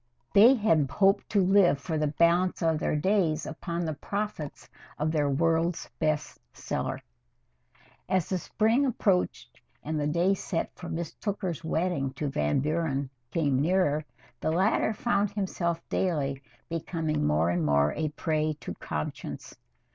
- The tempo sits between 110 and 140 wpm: No, average, 150 wpm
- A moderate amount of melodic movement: Yes, average, 4.1 semitones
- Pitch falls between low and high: Yes, medium, 165 Hz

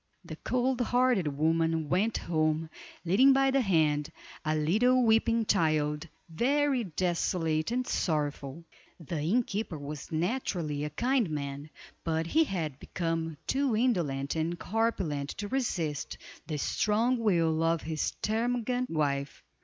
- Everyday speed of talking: No, slow, 130 wpm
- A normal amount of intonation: No, wide, 7.0 semitones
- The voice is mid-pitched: Yes, medium, 170 Hz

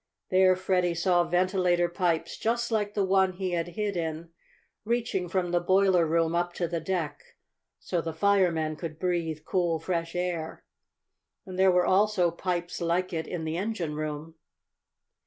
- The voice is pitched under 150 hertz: No, medium, 175 Hz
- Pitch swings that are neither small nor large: No, narrow, 2.1 semitones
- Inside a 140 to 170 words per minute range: Yes, average, 155 wpm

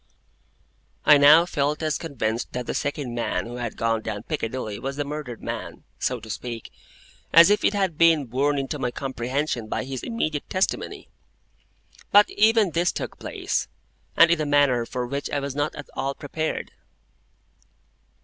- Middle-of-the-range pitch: Yes, medium, 145 Hz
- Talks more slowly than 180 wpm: Yes, average, 170 wpm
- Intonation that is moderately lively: Yes, average, 4.3 semitones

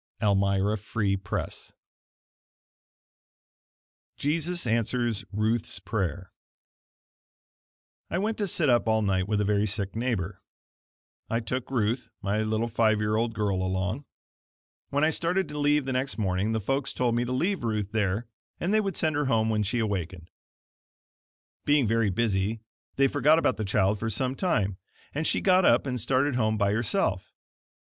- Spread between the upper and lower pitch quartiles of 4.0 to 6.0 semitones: Yes, average, 4.6 semitones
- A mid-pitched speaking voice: No, low, 115 Hz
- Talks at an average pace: Yes, average, 160 wpm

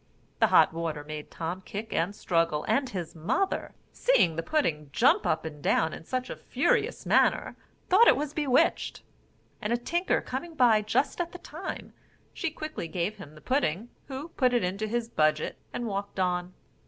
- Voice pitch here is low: No, high, 210 Hz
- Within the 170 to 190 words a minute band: Yes, average, 180 wpm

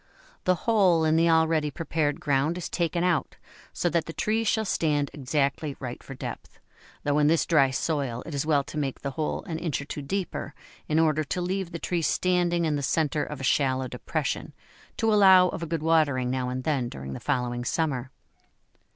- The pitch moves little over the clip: No, average, 3.5 semitones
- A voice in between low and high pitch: Yes, medium, 155 Hz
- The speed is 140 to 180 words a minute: No, fast, 205 wpm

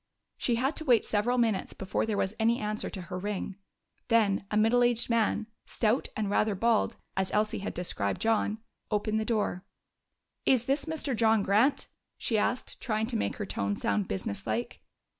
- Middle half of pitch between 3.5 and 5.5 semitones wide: No, average, 2.8 semitones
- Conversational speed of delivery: Yes, average, 180 wpm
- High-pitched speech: Yes, high, 215 Hz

